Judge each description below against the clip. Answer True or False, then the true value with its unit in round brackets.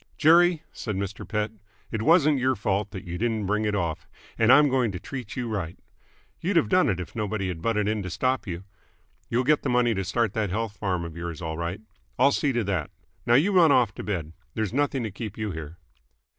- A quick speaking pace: True (225 wpm)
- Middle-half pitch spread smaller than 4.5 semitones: False (5.4 semitones)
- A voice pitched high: False (110 Hz)